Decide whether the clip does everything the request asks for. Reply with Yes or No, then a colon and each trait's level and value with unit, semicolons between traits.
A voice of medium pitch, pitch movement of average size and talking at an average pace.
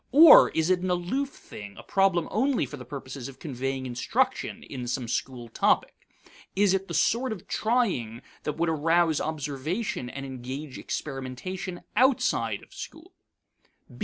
No: medium, 160 Hz; wide, 7.2 semitones; average, 150 wpm